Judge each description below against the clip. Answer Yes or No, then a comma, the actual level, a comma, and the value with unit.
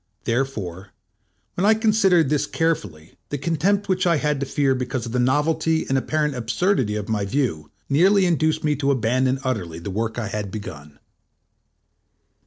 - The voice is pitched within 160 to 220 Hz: No, low, 135 Hz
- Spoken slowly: No, average, 165 wpm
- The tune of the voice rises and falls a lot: Yes, wide, 6.7 semitones